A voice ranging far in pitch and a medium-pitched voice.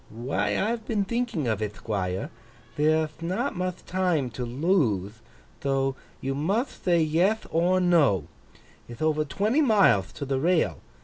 Yes: wide, 6.4 semitones; medium, 155 Hz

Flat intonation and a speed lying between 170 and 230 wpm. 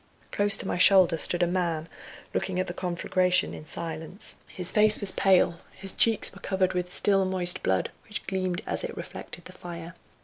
Yes: narrow, 1.7 semitones; average, 190 wpm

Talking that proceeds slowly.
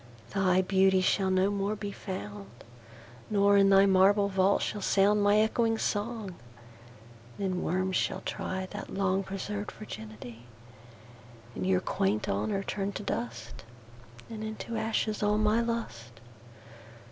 Yes: slow, 115 wpm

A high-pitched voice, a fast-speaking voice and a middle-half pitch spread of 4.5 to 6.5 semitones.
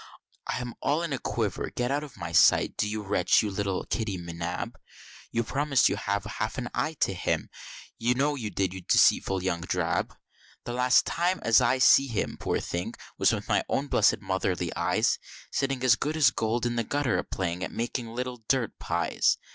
No: low, 115 Hz; fast, 210 wpm; average, 5.2 semitones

